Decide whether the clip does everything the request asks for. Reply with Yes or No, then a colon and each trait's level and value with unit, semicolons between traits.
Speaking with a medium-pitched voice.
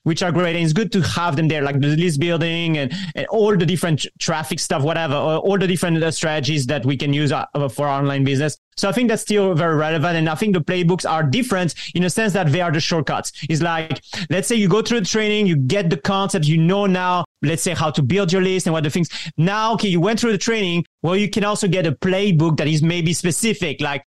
Yes: medium, 170 Hz